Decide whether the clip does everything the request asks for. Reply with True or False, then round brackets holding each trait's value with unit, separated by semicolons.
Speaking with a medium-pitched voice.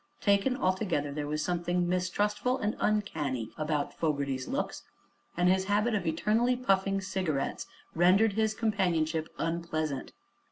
True (180 Hz)